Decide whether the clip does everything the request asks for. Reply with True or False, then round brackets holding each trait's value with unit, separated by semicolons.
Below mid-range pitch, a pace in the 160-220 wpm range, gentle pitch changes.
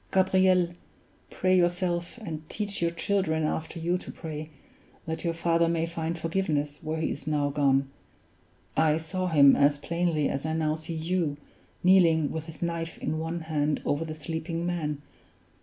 False (160 Hz; 165 wpm; 2.0 semitones)